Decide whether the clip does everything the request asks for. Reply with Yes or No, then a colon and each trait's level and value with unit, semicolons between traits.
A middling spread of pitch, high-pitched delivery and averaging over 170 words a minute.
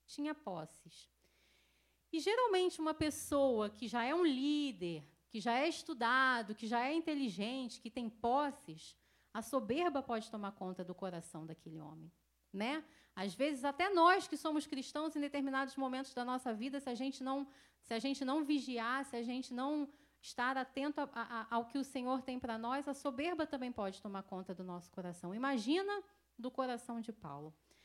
Yes: average, 4.6 semitones; very high, 255 Hz; average, 180 wpm